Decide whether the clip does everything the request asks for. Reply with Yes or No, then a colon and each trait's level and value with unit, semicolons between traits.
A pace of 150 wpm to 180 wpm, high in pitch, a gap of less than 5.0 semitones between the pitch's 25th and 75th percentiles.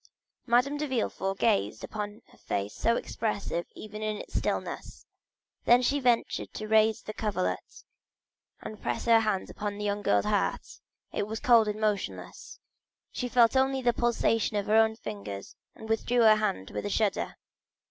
Yes: average, 170 wpm; high, 215 Hz; narrow, 2.4 semitones